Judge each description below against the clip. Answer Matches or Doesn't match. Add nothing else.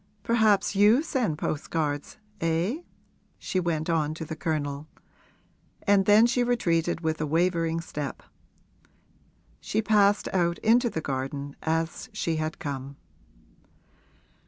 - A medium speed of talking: Doesn't match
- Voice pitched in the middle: Matches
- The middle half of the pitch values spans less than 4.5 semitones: Doesn't match